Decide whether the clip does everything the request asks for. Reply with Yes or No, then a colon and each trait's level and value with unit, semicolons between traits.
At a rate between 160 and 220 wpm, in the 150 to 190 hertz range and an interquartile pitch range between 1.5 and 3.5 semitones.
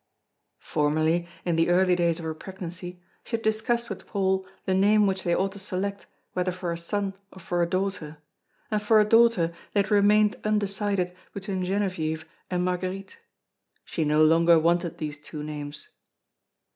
Yes: average, 170 wpm; medium, 185 Hz; average, 3.1 semitones